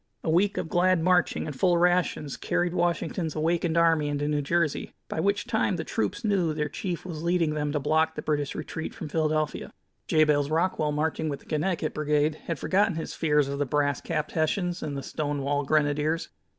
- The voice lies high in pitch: No, medium, 155 Hz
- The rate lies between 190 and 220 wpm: Yes, average, 195 wpm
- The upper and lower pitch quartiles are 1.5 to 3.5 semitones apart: Yes, average, 2.7 semitones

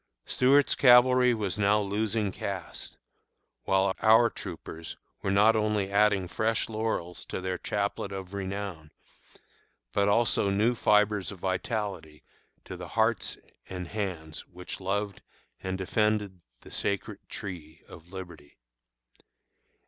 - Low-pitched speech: Yes, low, 100 Hz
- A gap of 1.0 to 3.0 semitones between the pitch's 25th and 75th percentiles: Yes, narrow, 2.6 semitones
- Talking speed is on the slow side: Yes, slow, 120 wpm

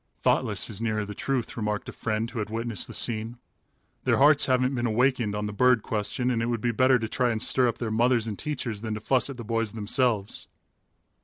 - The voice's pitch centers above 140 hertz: No, low, 115 Hz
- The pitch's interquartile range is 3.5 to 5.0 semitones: No, narrow, 2.6 semitones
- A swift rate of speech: Yes, fast, 230 wpm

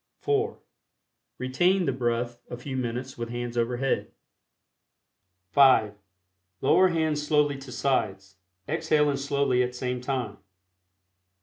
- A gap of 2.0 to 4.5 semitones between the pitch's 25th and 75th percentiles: Yes, average, 3.3 semitones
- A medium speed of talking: No, slow, 115 wpm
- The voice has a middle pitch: No, low, 130 Hz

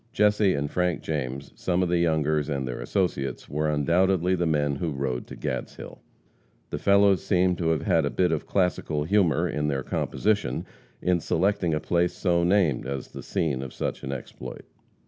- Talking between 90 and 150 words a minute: No, average, 185 wpm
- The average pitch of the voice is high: No, very low, 80 Hz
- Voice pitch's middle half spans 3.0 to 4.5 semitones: Yes, average, 4.0 semitones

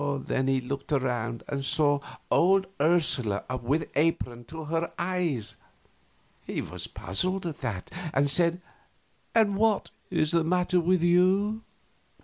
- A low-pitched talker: No, medium, 160 Hz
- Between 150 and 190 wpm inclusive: No, slow, 135 wpm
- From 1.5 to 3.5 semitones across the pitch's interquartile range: No, average, 5.1 semitones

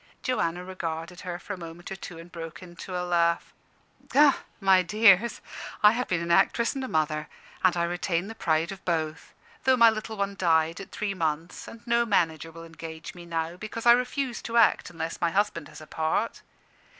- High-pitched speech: No, medium, 175 Hz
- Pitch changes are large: No, average, 4.2 semitones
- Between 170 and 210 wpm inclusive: Yes, average, 195 wpm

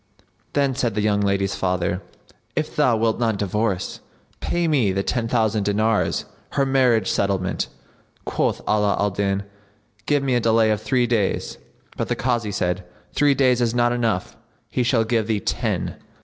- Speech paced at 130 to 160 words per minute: No, average, 170 wpm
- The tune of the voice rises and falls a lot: No, average, 3.3 semitones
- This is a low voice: Yes, low, 110 Hz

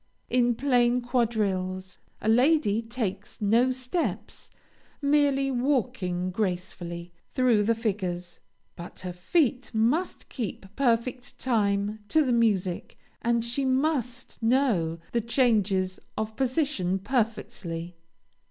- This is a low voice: No, high, 230 Hz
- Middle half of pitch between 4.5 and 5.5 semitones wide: Yes, average, 5.1 semitones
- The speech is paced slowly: Yes, slow, 105 wpm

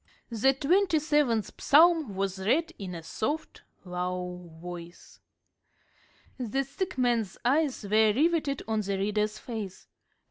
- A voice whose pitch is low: No, high, 220 Hz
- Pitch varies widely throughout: Yes, wide, 7.2 semitones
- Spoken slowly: Yes, slow, 120 wpm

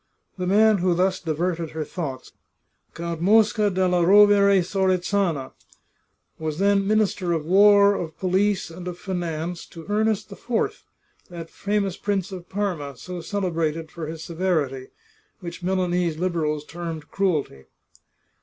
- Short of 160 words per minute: Yes, average, 140 wpm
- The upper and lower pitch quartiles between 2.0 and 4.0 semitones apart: Yes, average, 3.3 semitones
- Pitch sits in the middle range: Yes, medium, 180 Hz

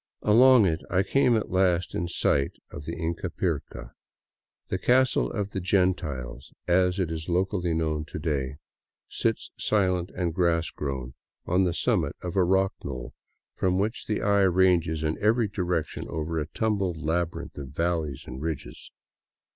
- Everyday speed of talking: Yes, average, 155 wpm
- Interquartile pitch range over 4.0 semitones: No, average, 3.4 semitones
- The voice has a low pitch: Yes, very low, 85 Hz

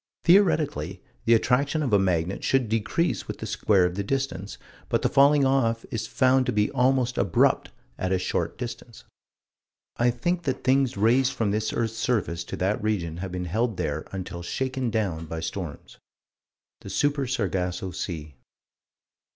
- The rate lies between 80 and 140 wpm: No, average, 165 wpm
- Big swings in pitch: Yes, wide, 6.1 semitones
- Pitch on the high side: No, low, 110 Hz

